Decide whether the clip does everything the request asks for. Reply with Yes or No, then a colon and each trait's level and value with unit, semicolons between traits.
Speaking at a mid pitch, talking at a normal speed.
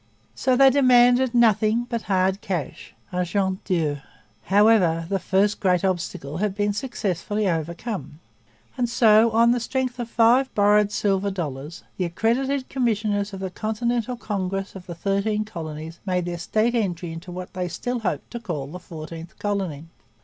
No: high, 200 Hz; average, 155 wpm